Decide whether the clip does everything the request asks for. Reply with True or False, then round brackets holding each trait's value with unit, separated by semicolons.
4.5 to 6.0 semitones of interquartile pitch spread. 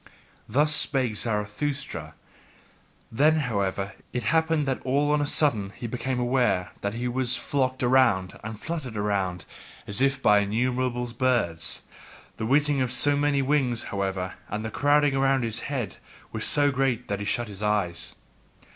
True (4.9 semitones)